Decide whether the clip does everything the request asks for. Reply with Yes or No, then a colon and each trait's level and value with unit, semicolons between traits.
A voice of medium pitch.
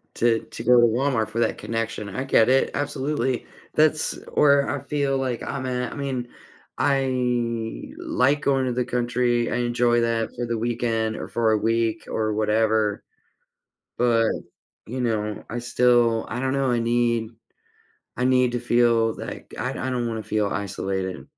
No: low, 120 Hz